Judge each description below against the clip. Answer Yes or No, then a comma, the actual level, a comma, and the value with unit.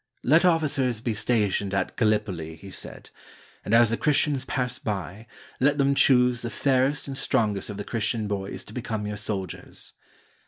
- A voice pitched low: Yes, low, 115 Hz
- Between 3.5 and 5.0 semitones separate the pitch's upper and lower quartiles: Yes, average, 4.4 semitones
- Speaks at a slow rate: No, average, 165 wpm